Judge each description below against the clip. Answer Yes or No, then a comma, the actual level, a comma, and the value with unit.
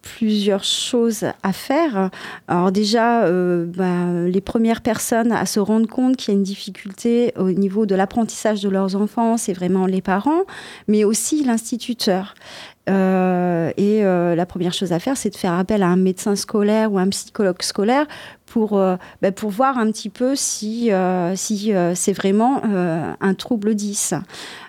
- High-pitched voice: Yes, high, 205 Hz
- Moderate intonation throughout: Yes, average, 3.3 semitones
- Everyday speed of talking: Yes, average, 175 wpm